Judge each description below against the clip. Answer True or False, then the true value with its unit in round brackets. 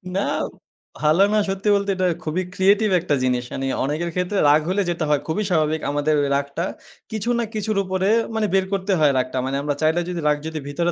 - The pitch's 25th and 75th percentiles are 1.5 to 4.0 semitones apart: False (4.6 semitones)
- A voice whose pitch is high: False (170 Hz)